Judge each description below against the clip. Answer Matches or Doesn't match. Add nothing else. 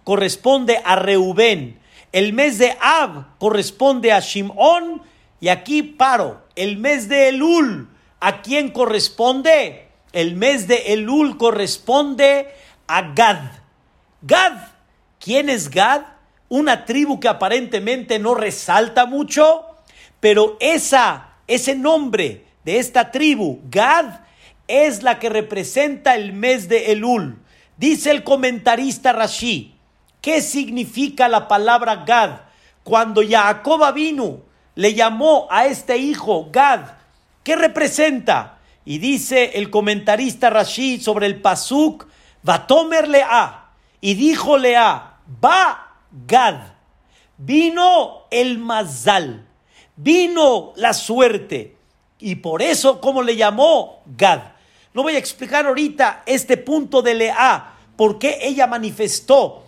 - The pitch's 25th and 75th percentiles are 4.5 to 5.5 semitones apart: Matches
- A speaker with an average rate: Doesn't match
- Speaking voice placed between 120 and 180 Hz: Doesn't match